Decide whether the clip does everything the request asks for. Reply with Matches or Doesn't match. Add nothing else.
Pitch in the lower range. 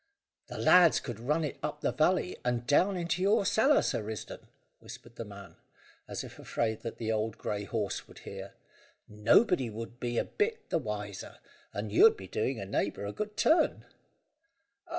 Matches